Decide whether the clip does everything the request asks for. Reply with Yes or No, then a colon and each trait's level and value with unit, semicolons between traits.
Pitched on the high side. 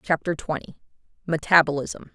No: medium, 155 Hz